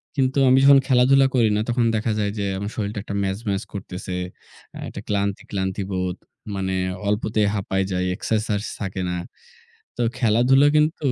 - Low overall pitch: Yes, low, 105 Hz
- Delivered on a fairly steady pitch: No, average, 4.2 semitones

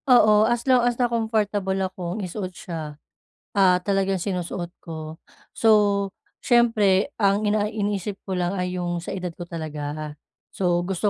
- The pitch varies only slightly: No, average, 3.3 semitones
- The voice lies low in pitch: No, high, 190 Hz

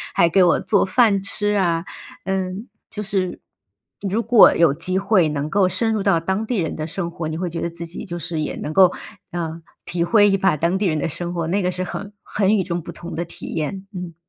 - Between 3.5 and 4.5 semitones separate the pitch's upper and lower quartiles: No, average, 2.8 semitones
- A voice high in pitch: No, medium, 180 Hz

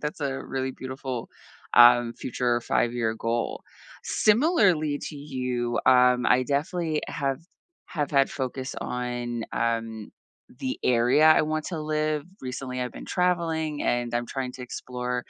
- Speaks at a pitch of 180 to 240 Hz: No, low, 130 Hz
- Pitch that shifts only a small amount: No, average, 3.8 semitones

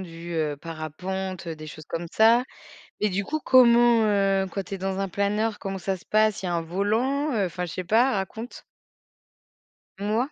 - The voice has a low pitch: No, high, 195 Hz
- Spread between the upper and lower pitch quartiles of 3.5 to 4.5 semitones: Yes, average, 3.9 semitones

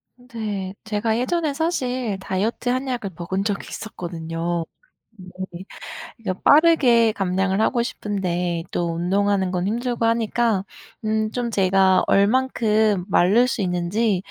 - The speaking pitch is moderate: No, high, 205 Hz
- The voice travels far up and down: No, average, 4.1 semitones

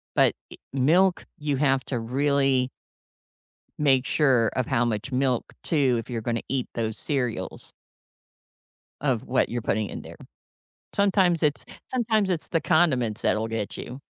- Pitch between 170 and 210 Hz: No, low, 135 Hz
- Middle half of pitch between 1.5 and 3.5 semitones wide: No, average, 4.1 semitones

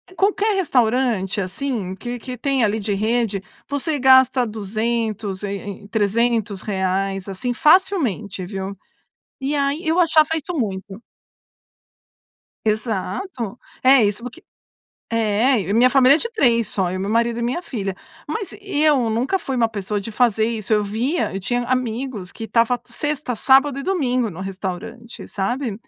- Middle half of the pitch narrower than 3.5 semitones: No, average, 4.8 semitones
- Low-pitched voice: No, high, 230 Hz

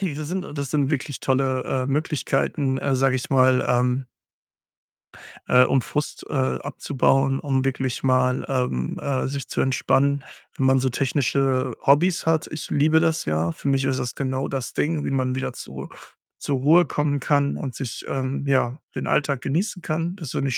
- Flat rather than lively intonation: Yes, narrow, 2.0 semitones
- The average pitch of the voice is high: No, low, 135 Hz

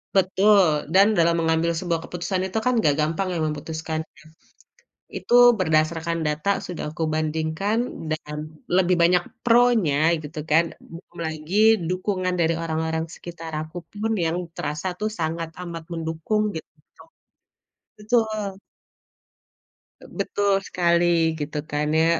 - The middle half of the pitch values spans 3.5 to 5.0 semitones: No, average, 3.0 semitones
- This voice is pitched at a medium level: Yes, medium, 170 Hz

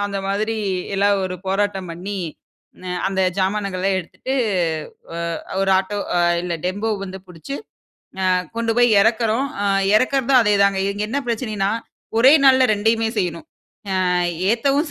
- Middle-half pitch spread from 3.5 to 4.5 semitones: No, average, 3.1 semitones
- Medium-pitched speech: No, high, 205 Hz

